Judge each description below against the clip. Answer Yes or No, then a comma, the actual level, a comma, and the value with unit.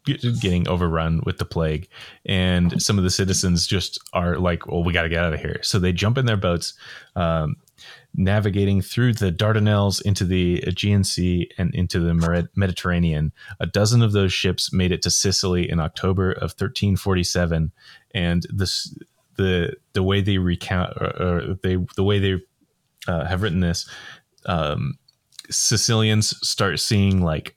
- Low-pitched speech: Yes, very low, 95 Hz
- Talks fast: No, average, 165 wpm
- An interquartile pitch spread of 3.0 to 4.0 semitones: No, narrow, 2.4 semitones